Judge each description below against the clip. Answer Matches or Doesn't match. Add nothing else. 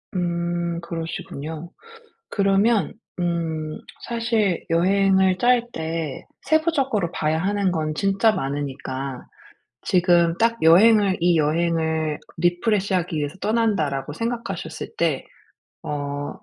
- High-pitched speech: Doesn't match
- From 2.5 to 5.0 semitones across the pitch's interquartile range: Matches